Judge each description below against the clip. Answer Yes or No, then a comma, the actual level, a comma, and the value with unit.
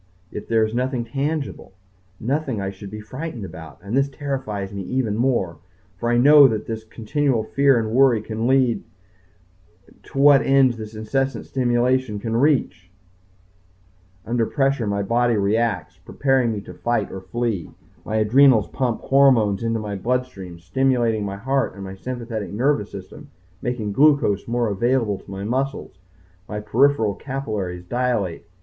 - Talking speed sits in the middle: Yes, average, 155 wpm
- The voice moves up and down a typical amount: Yes, average, 4.2 semitones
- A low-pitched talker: Yes, low, 115 Hz